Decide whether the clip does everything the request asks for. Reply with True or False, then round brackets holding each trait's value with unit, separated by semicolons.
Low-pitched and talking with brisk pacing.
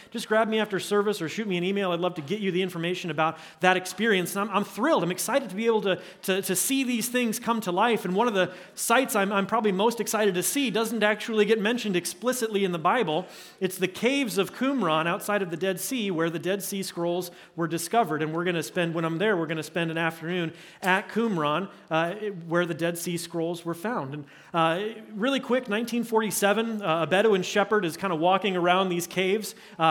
False (190 Hz; 235 wpm)